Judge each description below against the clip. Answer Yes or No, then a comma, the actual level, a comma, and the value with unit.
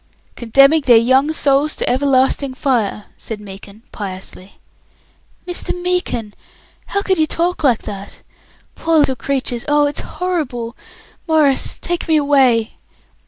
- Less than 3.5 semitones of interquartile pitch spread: No, average, 5.3 semitones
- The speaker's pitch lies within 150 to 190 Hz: No, very high, 275 Hz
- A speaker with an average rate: No, slow, 125 wpm